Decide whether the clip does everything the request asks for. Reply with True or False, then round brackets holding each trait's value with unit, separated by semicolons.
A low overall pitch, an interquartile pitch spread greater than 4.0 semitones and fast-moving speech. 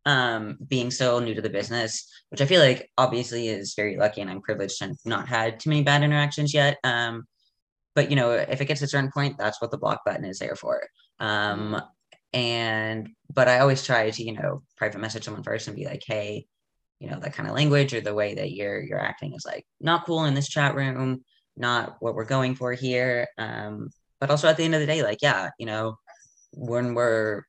True (125 Hz; 4.5 semitones; 225 wpm)